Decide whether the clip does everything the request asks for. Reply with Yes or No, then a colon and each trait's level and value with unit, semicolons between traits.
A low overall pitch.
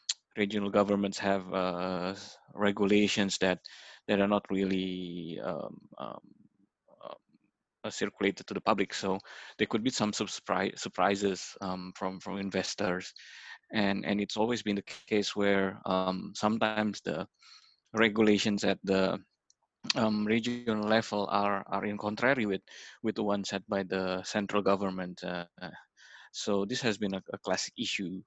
Yes: low, 100 Hz